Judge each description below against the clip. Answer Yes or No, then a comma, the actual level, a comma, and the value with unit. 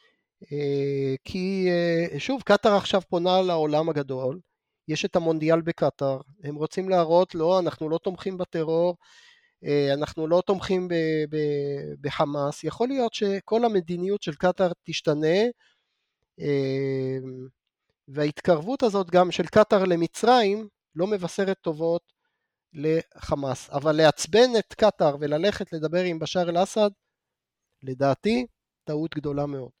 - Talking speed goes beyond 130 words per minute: No, average, 115 wpm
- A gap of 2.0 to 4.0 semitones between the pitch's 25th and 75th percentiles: No, average, 4.8 semitones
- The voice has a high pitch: No, medium, 170 Hz